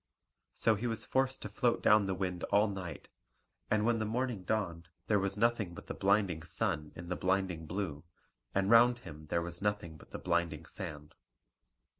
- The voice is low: Yes, very low, 95 Hz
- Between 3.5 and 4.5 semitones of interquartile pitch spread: Yes, average, 4.0 semitones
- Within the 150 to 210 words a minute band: Yes, average, 185 wpm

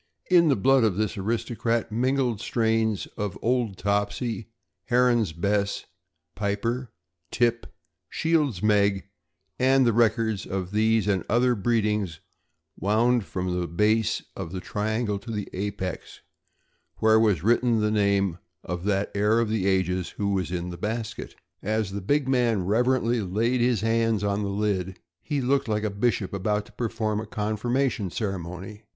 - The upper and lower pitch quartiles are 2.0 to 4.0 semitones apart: Yes, average, 2.9 semitones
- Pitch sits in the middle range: No, low, 105 Hz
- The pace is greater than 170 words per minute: No, average, 150 wpm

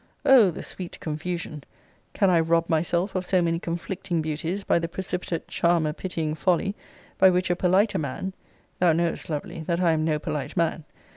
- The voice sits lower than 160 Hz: No, medium, 170 Hz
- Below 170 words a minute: No, average, 175 wpm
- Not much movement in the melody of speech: Yes, narrow, 2.3 semitones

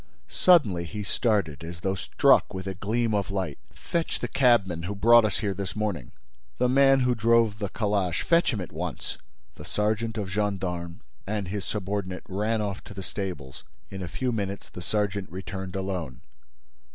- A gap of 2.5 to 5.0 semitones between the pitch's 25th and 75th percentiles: Yes, average, 2.8 semitones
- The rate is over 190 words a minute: No, average, 175 wpm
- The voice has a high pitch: No, low, 100 Hz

